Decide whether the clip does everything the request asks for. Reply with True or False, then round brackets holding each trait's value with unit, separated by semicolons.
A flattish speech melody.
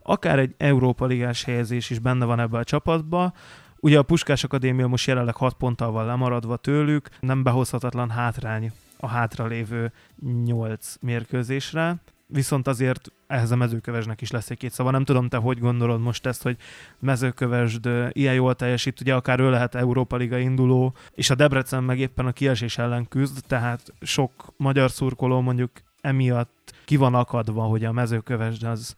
True (1.8 semitones)